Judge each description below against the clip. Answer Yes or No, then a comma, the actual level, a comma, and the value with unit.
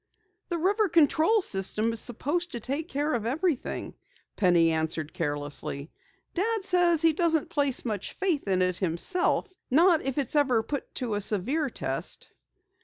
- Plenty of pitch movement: Yes, wide, 8.9 semitones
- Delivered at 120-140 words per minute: No, average, 155 wpm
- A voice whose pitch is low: No, very high, 280 Hz